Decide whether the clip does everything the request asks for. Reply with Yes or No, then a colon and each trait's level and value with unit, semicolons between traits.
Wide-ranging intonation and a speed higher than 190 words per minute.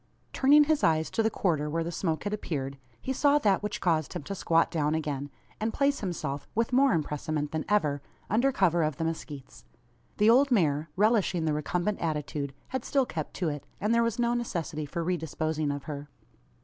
Yes: wide, 6.5 semitones; average, 200 wpm